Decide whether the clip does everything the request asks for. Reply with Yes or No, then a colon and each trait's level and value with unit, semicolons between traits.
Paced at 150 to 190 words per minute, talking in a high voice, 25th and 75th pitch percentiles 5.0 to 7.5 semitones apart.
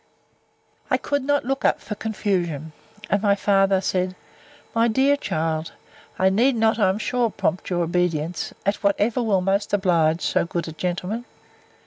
No: average, 160 wpm; high, 195 Hz; average, 4.0 semitones